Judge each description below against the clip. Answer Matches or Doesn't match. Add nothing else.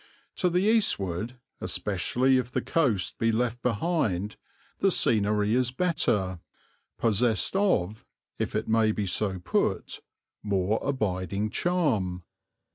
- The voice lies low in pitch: Matches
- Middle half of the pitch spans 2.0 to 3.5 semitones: Doesn't match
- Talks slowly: Matches